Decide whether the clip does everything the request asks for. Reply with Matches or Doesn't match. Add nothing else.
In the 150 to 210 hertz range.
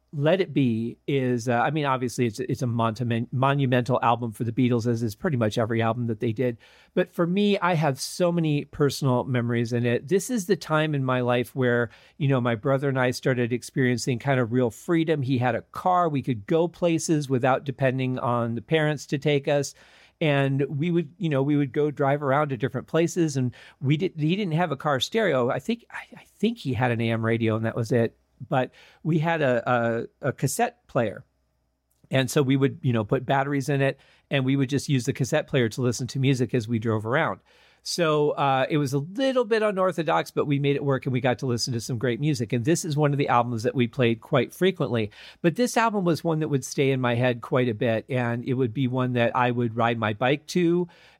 Doesn't match